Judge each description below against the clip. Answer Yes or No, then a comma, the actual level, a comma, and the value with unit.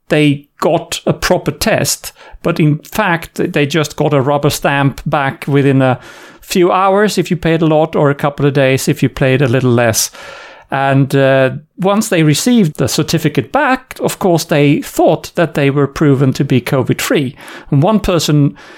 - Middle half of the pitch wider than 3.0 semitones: Yes, average, 3.6 semitones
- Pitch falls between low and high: Yes, medium, 150 Hz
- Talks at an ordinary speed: Yes, average, 185 wpm